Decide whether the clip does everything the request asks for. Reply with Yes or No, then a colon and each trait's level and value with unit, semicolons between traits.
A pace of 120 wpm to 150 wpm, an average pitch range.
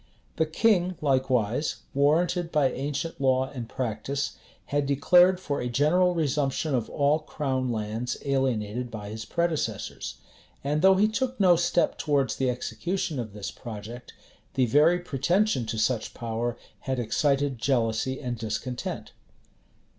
Yes: average, 140 wpm; average, 4.9 semitones